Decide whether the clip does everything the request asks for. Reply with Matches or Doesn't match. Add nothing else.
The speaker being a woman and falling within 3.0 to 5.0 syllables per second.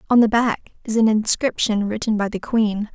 Matches